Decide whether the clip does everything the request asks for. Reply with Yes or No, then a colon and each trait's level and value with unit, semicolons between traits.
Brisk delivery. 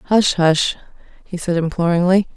No: slow, 100 wpm